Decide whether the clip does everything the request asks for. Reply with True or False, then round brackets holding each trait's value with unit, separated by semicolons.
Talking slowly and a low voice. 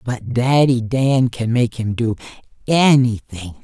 True (130 wpm; 120 Hz)